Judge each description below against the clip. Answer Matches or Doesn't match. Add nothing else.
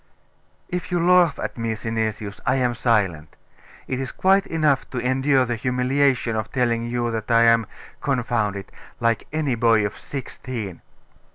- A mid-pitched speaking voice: Doesn't match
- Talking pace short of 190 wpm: Matches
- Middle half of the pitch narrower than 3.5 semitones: Matches